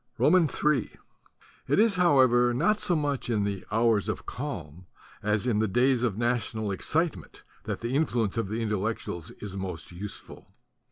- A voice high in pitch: No, low, 115 Hz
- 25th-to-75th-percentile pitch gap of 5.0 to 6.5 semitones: Yes, wide, 5.4 semitones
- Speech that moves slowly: No, average, 155 wpm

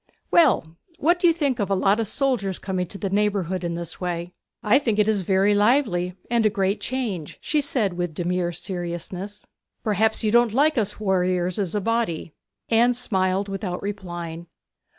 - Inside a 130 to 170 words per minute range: No, average, 180 wpm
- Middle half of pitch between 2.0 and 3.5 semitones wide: No, average, 4.0 semitones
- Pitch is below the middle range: No, high, 200 Hz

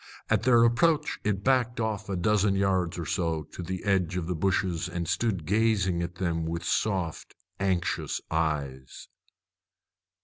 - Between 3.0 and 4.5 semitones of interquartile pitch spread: Yes, average, 3.9 semitones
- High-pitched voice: No, very low, 95 Hz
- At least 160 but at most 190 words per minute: No, average, 150 wpm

